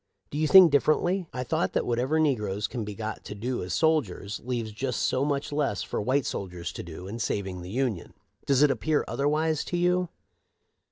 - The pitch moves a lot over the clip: Yes, wide, 6.5 semitones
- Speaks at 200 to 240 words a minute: Yes, fast, 205 wpm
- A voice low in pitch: Yes, low, 130 Hz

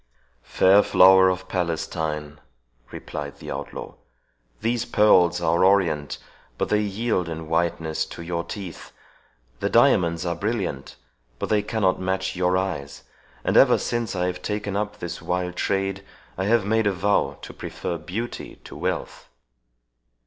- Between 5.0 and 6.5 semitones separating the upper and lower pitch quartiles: No, average, 3.2 semitones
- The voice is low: Yes, very low, 95 Hz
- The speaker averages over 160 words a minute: No, average, 145 wpm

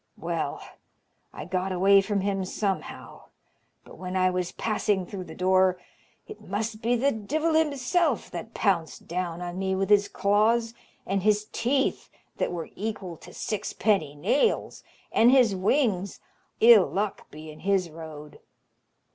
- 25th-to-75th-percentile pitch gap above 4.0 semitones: No, average, 3.5 semitones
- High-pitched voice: Yes, high, 200 Hz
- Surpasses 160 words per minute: No, average, 145 wpm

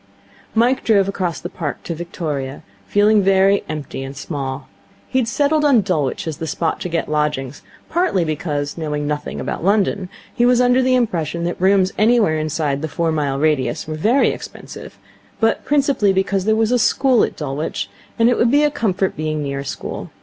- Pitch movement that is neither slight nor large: No, wide, 6.9 semitones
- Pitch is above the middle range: No, medium, 180 Hz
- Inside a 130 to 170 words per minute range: No, average, 190 wpm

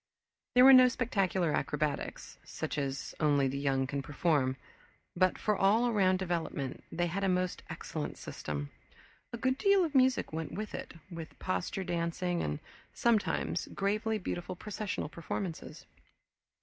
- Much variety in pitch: Yes, wide, 6.2 semitones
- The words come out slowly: No, average, 145 wpm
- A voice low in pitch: No, medium, 180 Hz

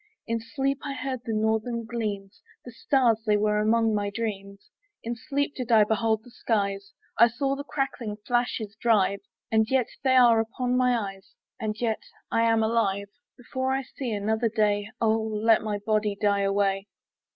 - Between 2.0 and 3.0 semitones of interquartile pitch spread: Yes, narrow, 2.6 semitones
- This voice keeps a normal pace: Yes, average, 175 wpm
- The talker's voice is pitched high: Yes, high, 225 Hz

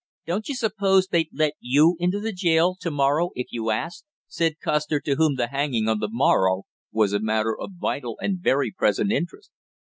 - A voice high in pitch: No, medium, 150 Hz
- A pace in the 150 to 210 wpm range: Yes, average, 200 wpm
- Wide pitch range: Yes, wide, 7.0 semitones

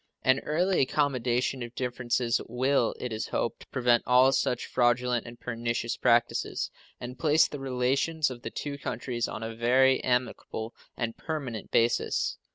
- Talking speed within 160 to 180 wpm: No, average, 150 wpm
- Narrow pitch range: Yes, narrow, 2.0 semitones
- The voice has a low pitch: Yes, low, 125 Hz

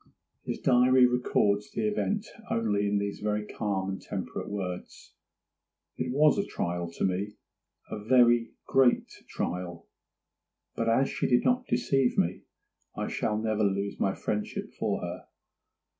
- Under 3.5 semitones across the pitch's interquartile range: No, average, 4.0 semitones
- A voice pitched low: Yes, low, 105 Hz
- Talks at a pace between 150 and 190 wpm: No, slow, 135 wpm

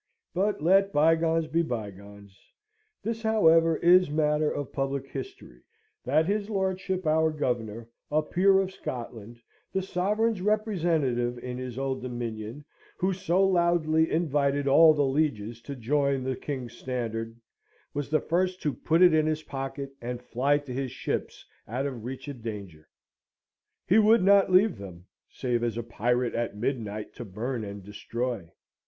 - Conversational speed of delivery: Yes, average, 155 wpm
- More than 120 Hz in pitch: Yes, medium, 140 Hz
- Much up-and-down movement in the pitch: Yes, wide, 6.3 semitones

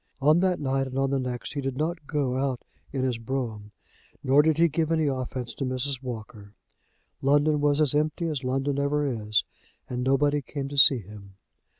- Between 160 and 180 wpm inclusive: No, average, 195 wpm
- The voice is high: No, low, 135 Hz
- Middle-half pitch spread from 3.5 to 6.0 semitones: No, narrow, 2.6 semitones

